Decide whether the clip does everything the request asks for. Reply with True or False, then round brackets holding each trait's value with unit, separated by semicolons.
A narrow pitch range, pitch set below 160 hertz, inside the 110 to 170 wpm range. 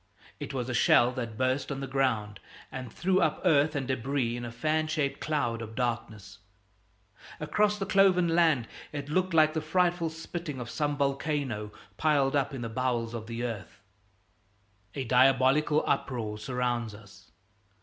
False (4.6 semitones; 135 Hz; 160 wpm)